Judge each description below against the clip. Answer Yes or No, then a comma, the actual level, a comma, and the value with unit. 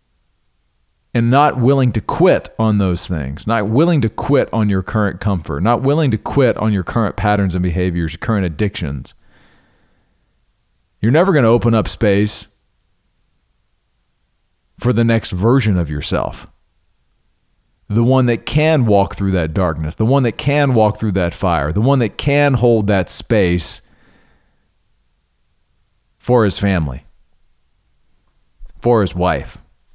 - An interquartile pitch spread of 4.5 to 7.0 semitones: Yes, average, 4.8 semitones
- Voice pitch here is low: Yes, low, 105 Hz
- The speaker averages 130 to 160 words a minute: Yes, average, 140 wpm